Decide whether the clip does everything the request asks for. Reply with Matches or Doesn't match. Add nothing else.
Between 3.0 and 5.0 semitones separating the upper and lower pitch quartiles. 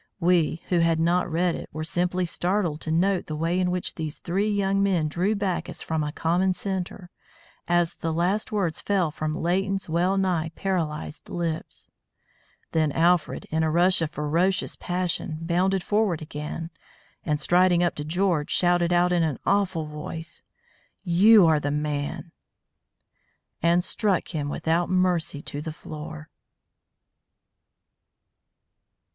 Doesn't match